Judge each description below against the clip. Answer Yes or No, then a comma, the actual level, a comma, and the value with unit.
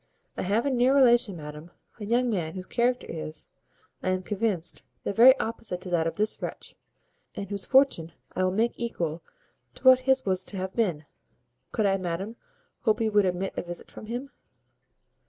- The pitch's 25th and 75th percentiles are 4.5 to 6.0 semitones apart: Yes, average, 4.9 semitones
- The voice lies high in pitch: Yes, high, 200 Hz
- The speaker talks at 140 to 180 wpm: No, average, 190 wpm